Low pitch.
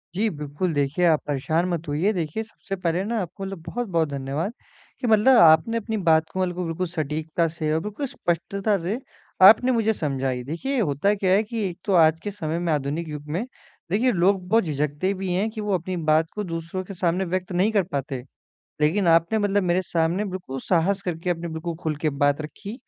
No: medium, 175 Hz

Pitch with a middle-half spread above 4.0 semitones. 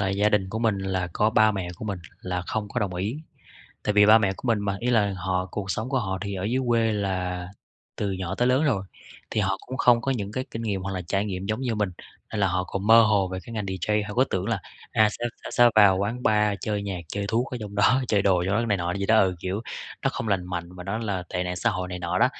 No: average, 2.8 semitones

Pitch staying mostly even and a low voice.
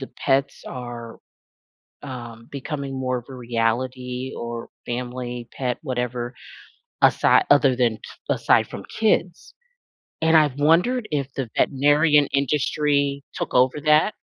No: average, 3.0 semitones; low, 130 Hz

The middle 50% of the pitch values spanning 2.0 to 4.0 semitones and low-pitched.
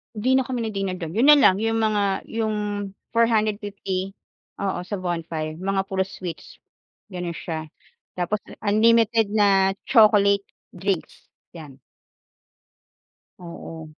No: average, 3.5 semitones; high, 200 Hz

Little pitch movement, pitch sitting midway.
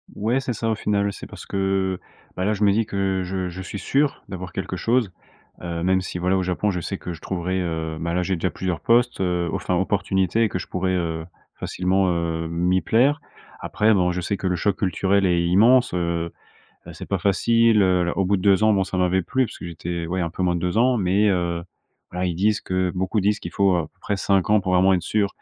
No: narrow, 2.3 semitones; very low, 95 Hz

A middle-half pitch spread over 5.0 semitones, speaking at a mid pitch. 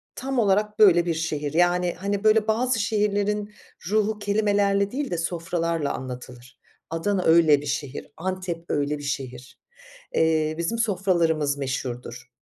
Yes: wide, 5.6 semitones; medium, 175 Hz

